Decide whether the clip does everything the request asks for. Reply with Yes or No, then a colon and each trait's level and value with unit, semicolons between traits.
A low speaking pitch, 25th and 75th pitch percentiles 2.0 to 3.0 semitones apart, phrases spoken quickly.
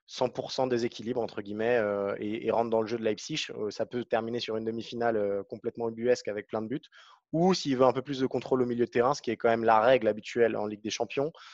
Yes: low, 115 Hz; narrow, 2.4 semitones; fast, 265 wpm